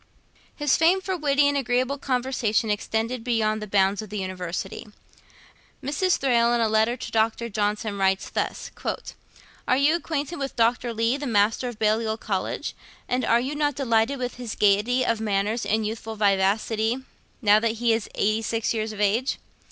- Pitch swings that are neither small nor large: Yes, average, 3.2 semitones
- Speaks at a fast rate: No, average, 175 wpm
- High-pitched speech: Yes, high, 225 Hz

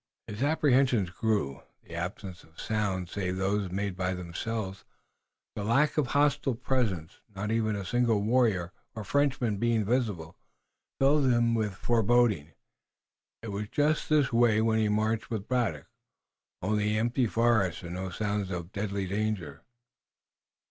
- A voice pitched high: No, low, 105 Hz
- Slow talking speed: No, average, 145 wpm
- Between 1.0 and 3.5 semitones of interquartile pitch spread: No, average, 4.0 semitones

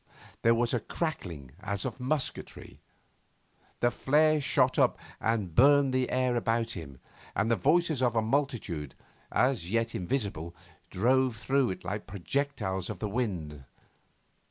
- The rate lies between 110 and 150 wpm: Yes, average, 140 wpm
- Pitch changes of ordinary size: No, wide, 5.7 semitones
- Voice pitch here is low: Yes, low, 115 Hz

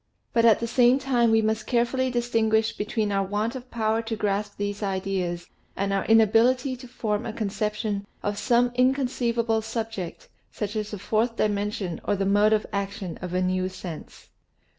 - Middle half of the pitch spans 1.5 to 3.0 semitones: Yes, average, 2.7 semitones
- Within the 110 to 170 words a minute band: No, average, 180 wpm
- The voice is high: Yes, high, 215 Hz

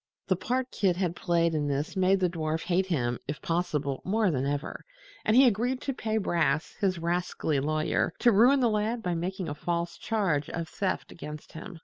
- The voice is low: No, medium, 175 Hz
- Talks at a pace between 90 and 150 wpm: No, average, 200 wpm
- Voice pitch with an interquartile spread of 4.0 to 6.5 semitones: Yes, average, 4.9 semitones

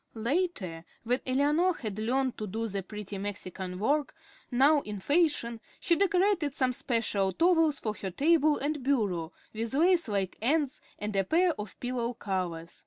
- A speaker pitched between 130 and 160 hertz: No, high, 245 Hz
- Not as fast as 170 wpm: Yes, average, 160 wpm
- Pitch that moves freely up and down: Yes, wide, 6.8 semitones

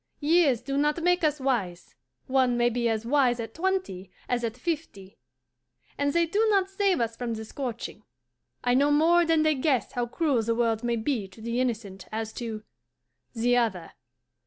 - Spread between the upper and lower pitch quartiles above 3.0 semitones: Yes, average, 5.1 semitones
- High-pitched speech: Yes, high, 245 Hz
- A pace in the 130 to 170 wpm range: No, average, 180 wpm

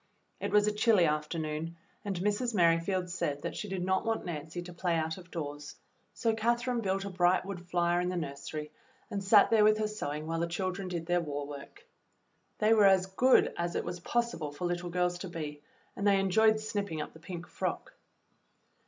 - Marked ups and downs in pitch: No, average, 3.7 semitones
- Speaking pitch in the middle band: Yes, medium, 180 Hz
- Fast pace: Yes, fast, 210 wpm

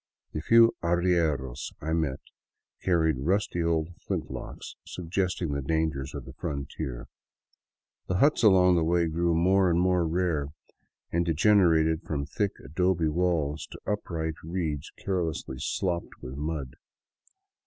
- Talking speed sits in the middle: No, slow, 130 wpm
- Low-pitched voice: Yes, very low, 85 Hz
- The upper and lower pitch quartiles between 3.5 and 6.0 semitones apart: No, average, 2.9 semitones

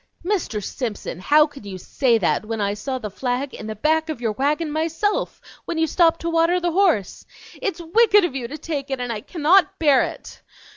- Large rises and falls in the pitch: Yes, wide, 6.1 semitones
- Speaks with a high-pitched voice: Yes, very high, 295 Hz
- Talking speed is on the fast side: Yes, fast, 210 wpm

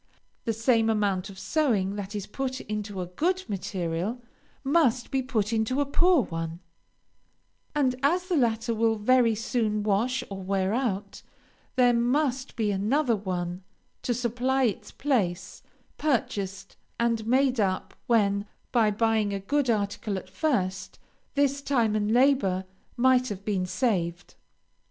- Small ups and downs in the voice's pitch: No, average, 4.6 semitones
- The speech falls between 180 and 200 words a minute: No, average, 140 wpm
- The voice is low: No, high, 225 Hz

